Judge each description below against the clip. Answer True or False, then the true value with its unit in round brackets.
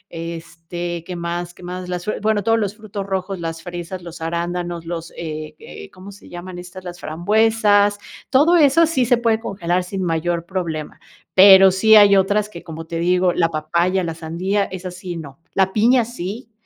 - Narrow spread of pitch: False (3.2 semitones)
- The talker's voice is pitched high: False (180 Hz)